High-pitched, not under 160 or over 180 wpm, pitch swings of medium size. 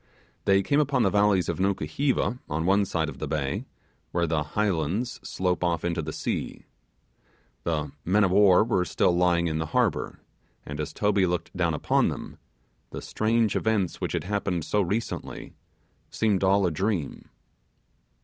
No: very low, 90 Hz; average, 165 wpm; average, 4.0 semitones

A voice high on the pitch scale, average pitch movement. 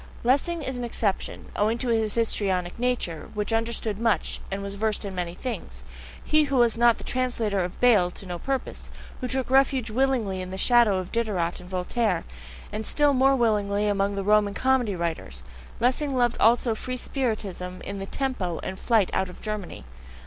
Yes: high, 220 Hz; average, 4.4 semitones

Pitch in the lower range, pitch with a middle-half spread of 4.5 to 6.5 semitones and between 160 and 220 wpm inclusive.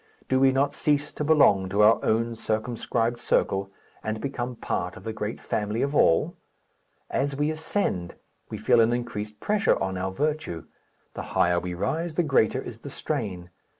Yes: low, 115 Hz; wide, 5.5 semitones; average, 175 wpm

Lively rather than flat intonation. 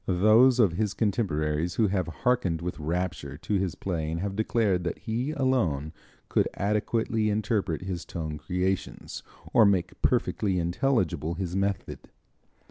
No: average, 4.3 semitones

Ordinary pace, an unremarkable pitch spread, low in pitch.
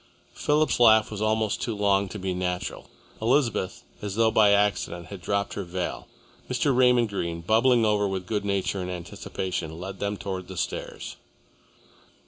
Yes: average, 160 wpm; average, 3.1 semitones; low, 100 Hz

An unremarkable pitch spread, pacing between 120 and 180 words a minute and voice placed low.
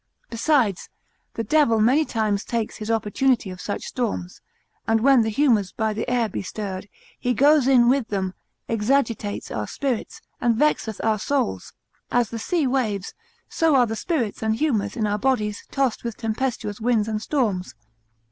No: average, 3.7 semitones; average, 165 wpm; high, 225 Hz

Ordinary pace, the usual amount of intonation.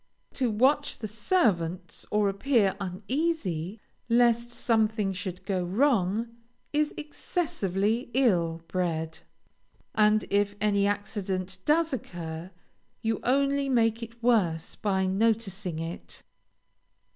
No: slow, 105 wpm; average, 4.3 semitones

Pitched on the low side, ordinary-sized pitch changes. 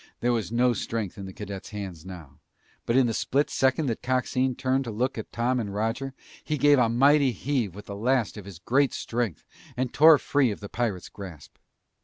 Yes: low, 120 Hz; average, 4.3 semitones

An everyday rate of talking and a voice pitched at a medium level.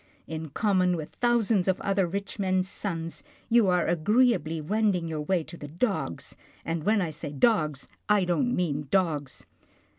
Yes: average, 160 wpm; medium, 180 Hz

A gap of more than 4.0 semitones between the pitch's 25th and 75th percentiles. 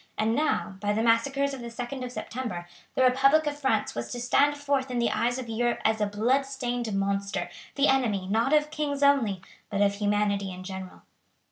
Yes: average, 4.8 semitones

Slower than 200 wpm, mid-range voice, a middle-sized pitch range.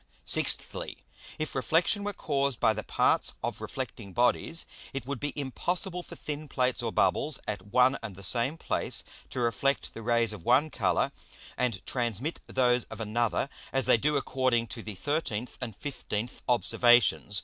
No: average, 165 wpm; low, 125 Hz; average, 3.9 semitones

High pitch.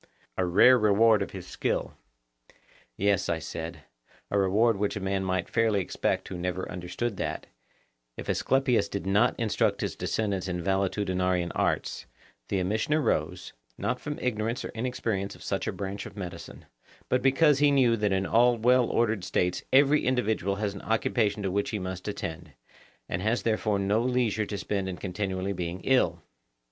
No: low, 100 Hz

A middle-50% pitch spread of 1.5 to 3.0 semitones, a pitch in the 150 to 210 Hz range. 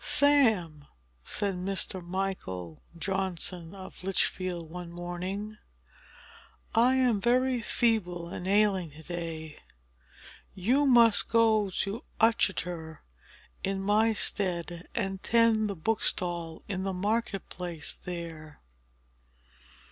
No: average, 3.9 semitones; high, 190 Hz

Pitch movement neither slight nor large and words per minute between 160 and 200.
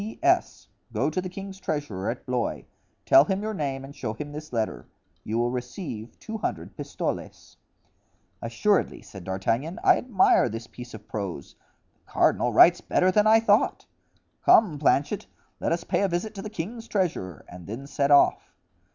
No: wide, 9.0 semitones; average, 170 wpm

